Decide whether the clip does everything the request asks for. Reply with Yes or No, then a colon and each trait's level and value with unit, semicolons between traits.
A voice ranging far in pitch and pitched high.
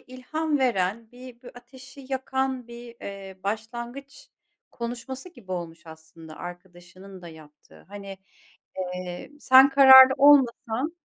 Yes: wide, 6.3 semitones; high, 235 Hz